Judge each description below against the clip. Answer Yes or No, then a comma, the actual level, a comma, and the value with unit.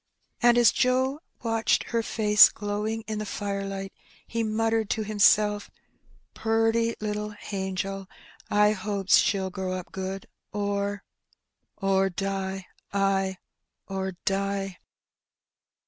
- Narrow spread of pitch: Yes, narrow, 2.0 semitones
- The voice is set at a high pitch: Yes, high, 205 Hz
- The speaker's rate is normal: No, slow, 120 wpm